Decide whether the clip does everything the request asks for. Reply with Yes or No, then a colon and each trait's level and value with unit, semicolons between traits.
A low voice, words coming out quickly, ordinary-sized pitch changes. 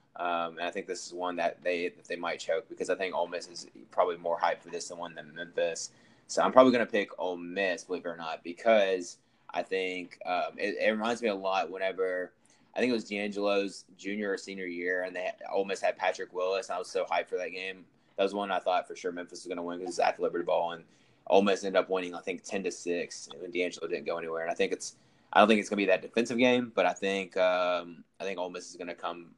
Yes: very low, 95 Hz; fast, 275 wpm; average, 4.2 semitones